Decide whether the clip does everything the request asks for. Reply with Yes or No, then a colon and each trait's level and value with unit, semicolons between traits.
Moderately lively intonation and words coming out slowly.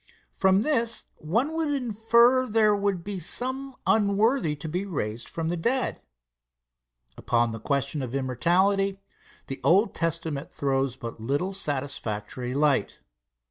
No: wide, 8.2 semitones; slow, 130 wpm